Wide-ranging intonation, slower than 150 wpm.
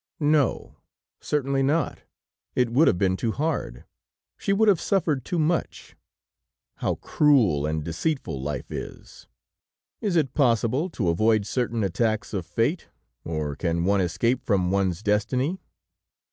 Yes: wide, 8.4 semitones; slow, 135 wpm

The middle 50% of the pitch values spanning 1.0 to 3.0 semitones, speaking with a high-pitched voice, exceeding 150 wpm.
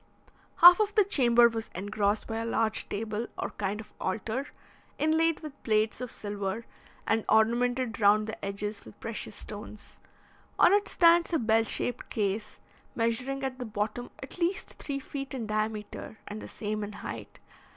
No: average, 3.9 semitones; high, 225 Hz; average, 165 wpm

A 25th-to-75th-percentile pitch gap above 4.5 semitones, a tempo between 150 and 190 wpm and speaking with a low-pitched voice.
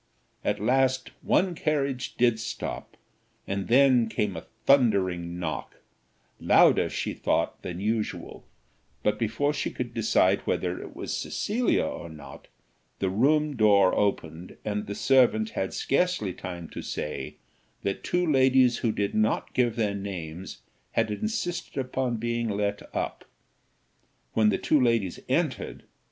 No: average, 4.9 semitones; average, 140 wpm; low, 110 Hz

